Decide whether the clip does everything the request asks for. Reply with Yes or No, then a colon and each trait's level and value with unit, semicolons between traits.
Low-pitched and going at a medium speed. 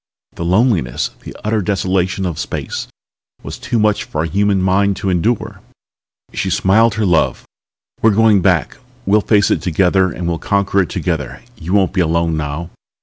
Yes: very low, 95 Hz; average, 170 wpm